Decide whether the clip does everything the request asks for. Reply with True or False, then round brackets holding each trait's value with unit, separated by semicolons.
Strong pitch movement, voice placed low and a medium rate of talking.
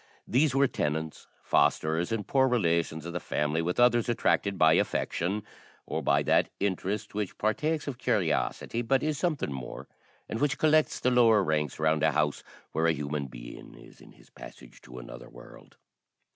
True (7.8 semitones; 95 Hz; 170 wpm)